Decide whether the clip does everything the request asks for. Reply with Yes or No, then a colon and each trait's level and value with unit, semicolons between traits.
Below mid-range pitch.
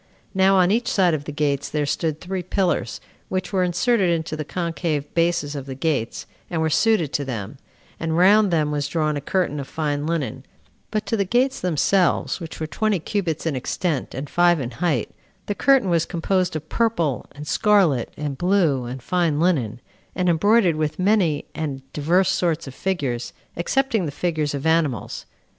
No: medium, 165 Hz